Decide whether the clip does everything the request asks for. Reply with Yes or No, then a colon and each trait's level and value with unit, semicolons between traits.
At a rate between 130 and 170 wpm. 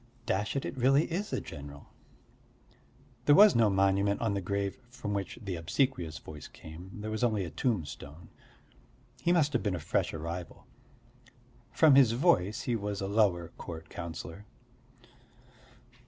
Yes: average, 155 wpm